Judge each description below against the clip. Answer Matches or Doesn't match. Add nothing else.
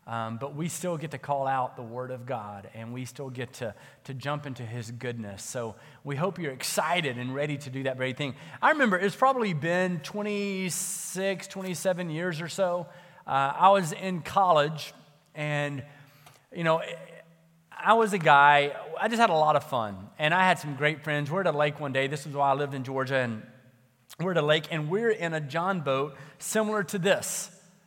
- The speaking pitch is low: Doesn't match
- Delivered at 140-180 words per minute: Doesn't match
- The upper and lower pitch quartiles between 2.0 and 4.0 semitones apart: Doesn't match